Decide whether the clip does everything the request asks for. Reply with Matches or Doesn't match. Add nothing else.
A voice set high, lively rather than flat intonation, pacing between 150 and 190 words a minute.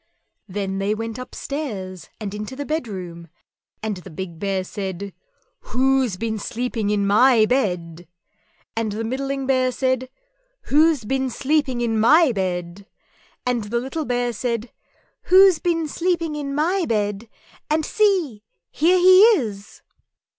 Doesn't match